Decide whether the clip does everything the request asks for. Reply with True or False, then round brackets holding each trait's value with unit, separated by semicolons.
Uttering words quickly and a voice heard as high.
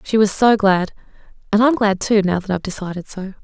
True (210 wpm; 200 Hz)